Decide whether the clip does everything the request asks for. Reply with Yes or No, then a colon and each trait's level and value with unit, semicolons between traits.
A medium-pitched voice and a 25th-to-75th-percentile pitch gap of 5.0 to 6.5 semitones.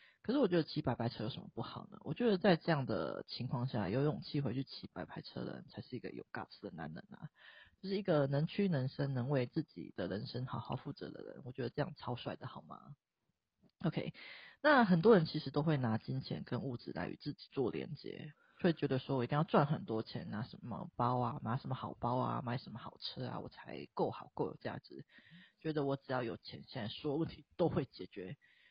Yes: medium, 145 Hz; wide, 5.5 semitones